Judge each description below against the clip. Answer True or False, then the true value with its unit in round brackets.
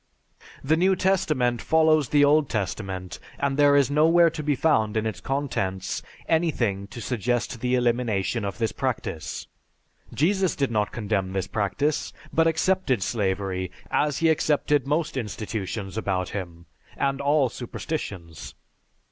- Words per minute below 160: True (140 wpm)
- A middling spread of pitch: False (7.0 semitones)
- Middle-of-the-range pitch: False (125 Hz)